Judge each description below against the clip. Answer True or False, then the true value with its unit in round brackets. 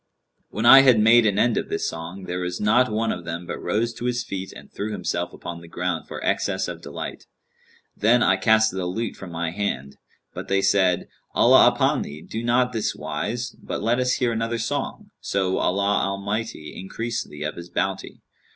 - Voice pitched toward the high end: False (100 Hz)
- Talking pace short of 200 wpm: False (205 wpm)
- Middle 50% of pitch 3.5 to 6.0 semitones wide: True (4.5 semitones)